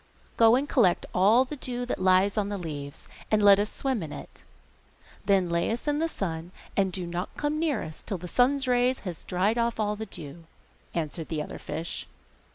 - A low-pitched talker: No, high, 200 Hz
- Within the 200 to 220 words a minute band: Yes, fast, 205 wpm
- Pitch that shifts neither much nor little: No, wide, 6.1 semitones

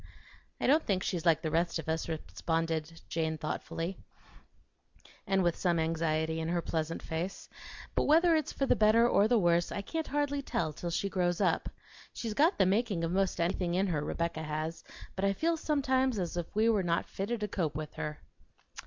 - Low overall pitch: No, medium, 175 Hz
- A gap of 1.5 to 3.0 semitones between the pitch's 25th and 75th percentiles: No, average, 4.9 semitones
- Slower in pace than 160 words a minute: No, average, 195 wpm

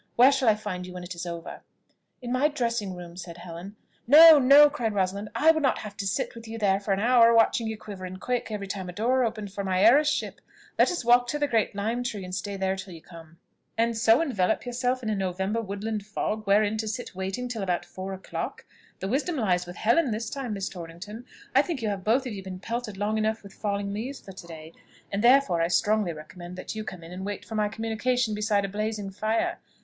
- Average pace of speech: No, fast, 240 wpm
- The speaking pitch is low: No, high, 210 Hz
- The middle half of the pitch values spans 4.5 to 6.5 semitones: No, average, 3.8 semitones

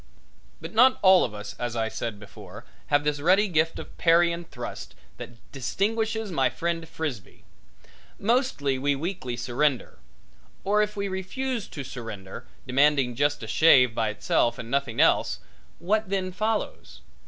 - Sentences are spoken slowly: No, average, 155 wpm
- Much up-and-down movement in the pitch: Yes, wide, 7.8 semitones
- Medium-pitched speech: Yes, medium, 150 Hz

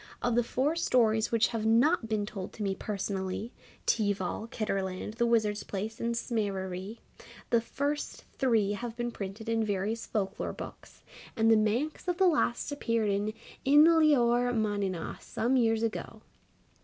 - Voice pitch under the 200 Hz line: No, high, 225 Hz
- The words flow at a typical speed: Yes, average, 155 wpm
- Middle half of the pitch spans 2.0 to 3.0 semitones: Yes, average, 2.7 semitones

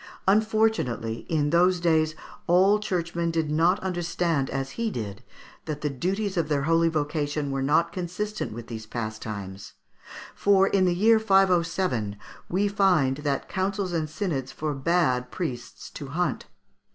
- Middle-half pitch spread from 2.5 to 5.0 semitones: No, wide, 5.4 semitones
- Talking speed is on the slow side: No, average, 145 wpm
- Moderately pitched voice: Yes, medium, 165 Hz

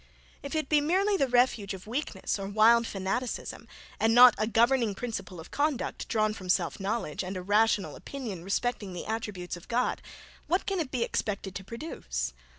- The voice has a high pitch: Yes, high, 220 Hz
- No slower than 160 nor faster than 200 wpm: Yes, average, 180 wpm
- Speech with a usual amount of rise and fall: Yes, average, 4.5 semitones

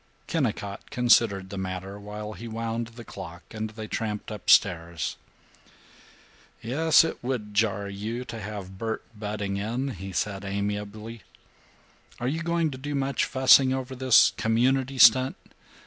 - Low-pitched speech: Yes, low, 110 Hz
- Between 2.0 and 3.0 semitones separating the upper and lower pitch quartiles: No, average, 4.1 semitones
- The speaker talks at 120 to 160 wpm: Yes, average, 145 wpm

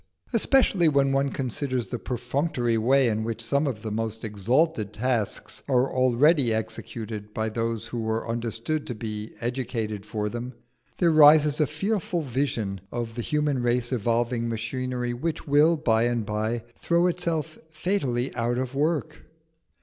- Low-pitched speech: Yes, low, 120 Hz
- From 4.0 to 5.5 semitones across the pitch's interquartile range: Yes, average, 4.3 semitones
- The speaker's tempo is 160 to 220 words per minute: No, average, 150 wpm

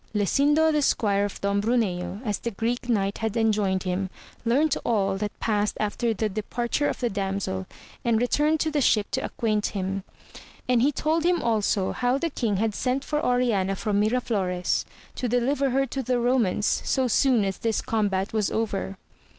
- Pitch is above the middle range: Yes, high, 225 Hz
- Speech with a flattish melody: No, average, 4.0 semitones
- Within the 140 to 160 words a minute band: No, average, 180 wpm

